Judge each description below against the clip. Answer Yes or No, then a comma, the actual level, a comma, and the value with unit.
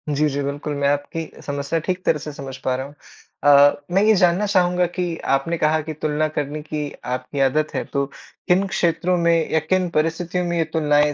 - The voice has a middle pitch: Yes, medium, 155 Hz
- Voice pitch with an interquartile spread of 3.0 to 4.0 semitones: Yes, average, 3.4 semitones